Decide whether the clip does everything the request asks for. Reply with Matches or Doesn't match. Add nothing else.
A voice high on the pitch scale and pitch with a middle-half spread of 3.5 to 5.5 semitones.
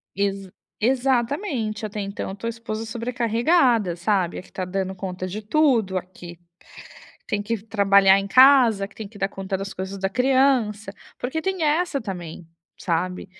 Matches